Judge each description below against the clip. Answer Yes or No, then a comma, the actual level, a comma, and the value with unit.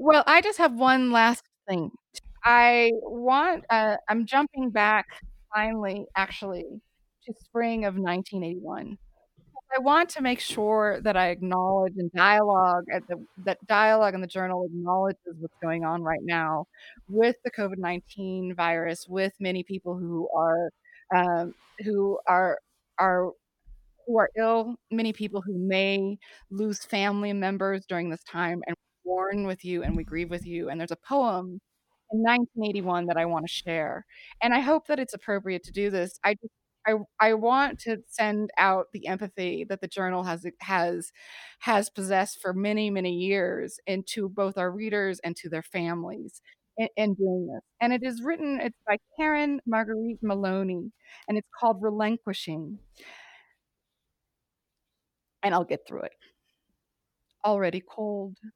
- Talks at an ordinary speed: Yes, average, 155 wpm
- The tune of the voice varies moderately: Yes, average, 3.7 semitones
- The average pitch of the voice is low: No, high, 200 Hz